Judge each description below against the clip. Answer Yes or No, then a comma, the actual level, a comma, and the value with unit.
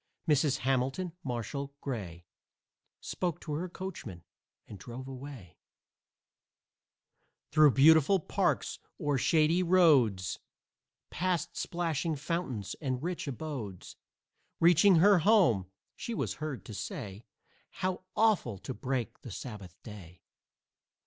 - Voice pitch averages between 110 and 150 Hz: Yes, medium, 140 Hz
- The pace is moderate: No, slow, 110 wpm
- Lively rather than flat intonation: Yes, wide, 6.5 semitones